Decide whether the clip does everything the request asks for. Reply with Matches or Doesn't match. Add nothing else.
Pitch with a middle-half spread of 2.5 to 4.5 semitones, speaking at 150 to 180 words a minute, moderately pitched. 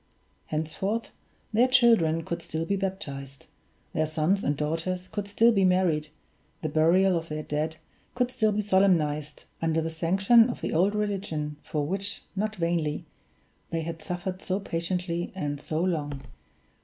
Matches